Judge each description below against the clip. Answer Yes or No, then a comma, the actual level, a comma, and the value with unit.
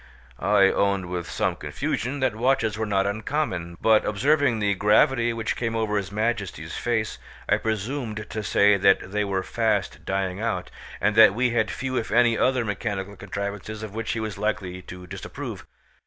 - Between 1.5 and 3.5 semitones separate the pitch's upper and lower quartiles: Yes, average, 2.8 semitones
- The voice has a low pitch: Yes, low, 105 Hz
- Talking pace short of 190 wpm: Yes, average, 175 wpm